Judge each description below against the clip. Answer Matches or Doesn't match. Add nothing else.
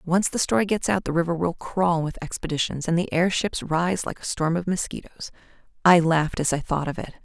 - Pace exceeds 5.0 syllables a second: Matches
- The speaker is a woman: Matches